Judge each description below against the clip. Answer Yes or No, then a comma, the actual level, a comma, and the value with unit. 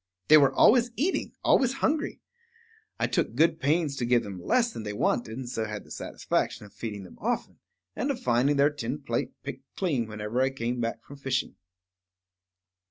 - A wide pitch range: Yes, wide, 6.1 semitones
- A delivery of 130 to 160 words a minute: No, average, 185 wpm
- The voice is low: Yes, low, 130 Hz